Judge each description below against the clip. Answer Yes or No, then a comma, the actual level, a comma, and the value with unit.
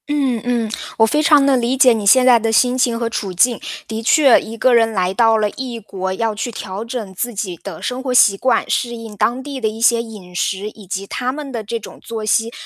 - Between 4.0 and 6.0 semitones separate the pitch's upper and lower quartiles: No, average, 2.8 semitones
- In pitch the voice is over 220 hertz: Yes, high, 230 Hz